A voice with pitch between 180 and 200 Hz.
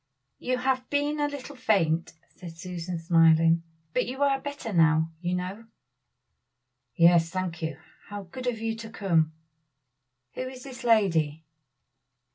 Yes: high, 190 Hz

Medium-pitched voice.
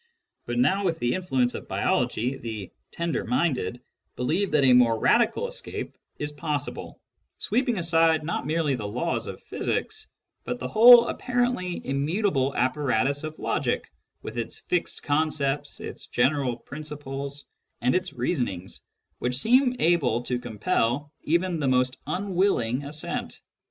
Yes: medium, 145 Hz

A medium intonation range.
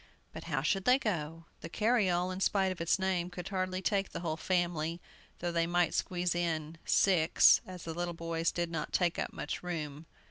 No: narrow, 2.0 semitones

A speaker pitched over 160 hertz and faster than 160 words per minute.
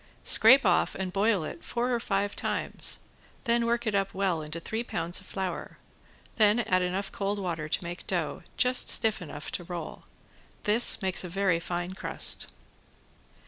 Yes: high, 190 Hz; average, 170 wpm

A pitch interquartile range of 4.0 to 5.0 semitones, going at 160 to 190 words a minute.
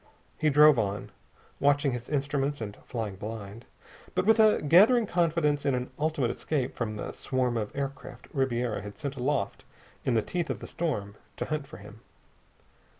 Yes: average, 4.7 semitones; average, 170 wpm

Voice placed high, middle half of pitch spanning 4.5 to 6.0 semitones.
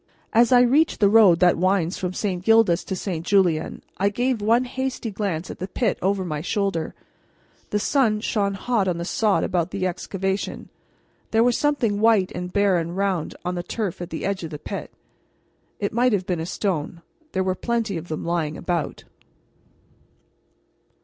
No: high, 195 Hz; average, 3.9 semitones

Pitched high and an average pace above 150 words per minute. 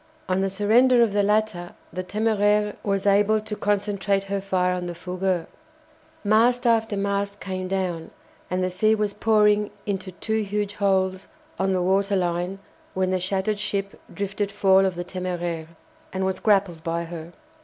Yes: high, 195 Hz; average, 165 wpm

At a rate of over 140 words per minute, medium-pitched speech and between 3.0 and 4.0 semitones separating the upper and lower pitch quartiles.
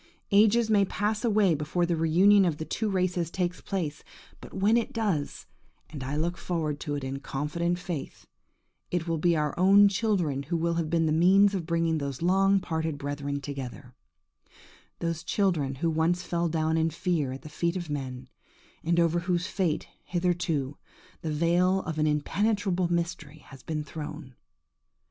Yes: average, 170 wpm; medium, 170 Hz; average, 3.5 semitones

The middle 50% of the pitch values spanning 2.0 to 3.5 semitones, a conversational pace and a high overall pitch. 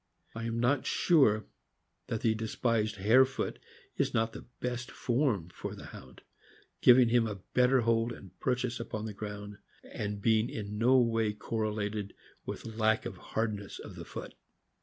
No: narrow, 2.4 semitones; average, 160 wpm; low, 115 Hz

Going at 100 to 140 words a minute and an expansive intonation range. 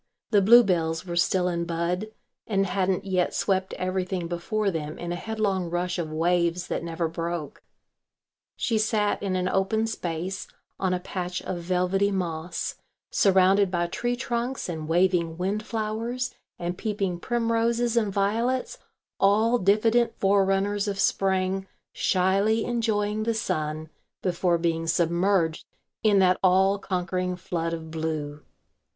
No: slow, 135 wpm; average, 3.3 semitones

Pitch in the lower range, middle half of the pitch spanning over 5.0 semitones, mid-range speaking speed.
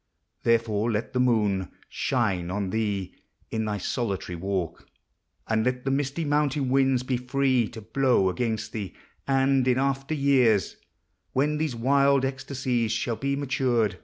No: low, 125 Hz; average, 4.0 semitones; average, 160 wpm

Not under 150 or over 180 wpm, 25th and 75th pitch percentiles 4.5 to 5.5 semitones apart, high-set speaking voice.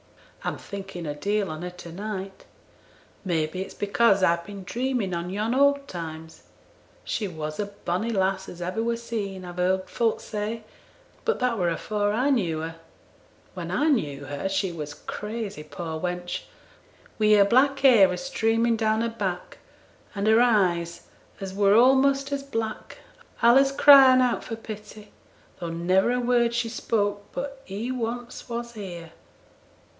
Yes: average, 160 wpm; average, 4.8 semitones; high, 205 Hz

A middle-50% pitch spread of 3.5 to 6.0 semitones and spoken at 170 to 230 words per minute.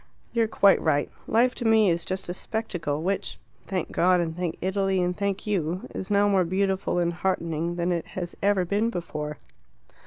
No: average, 2.8 semitones; average, 190 wpm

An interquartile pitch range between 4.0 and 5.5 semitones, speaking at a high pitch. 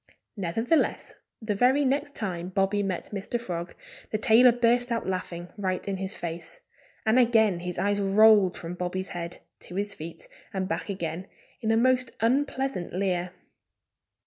Yes: average, 4.5 semitones; high, 200 Hz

